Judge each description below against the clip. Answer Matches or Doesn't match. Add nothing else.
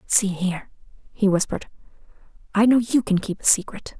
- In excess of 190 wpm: Doesn't match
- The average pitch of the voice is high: Matches